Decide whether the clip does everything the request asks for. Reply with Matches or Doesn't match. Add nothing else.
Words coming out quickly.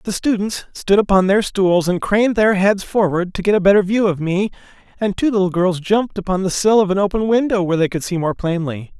Matches